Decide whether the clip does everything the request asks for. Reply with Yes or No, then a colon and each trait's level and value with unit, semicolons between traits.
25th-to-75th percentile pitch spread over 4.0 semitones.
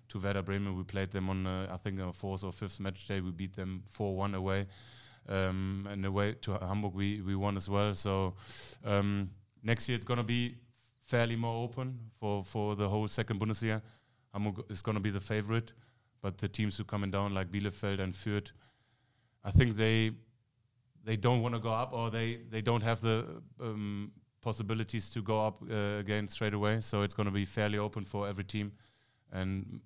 No: narrow, 2.6 semitones